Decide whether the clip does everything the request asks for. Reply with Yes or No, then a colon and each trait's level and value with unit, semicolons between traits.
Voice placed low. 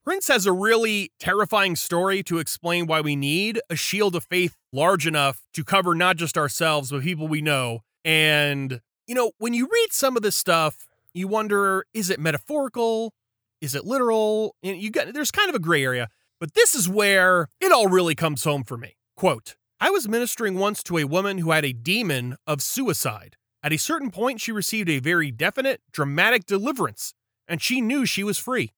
No: medium, 180 Hz